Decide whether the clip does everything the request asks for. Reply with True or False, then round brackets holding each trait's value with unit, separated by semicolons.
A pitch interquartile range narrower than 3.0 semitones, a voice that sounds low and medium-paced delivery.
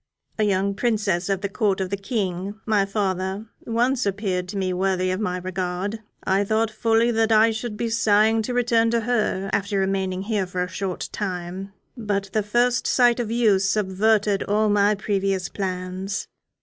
False (2.6 semitones; 200 Hz; 175 wpm)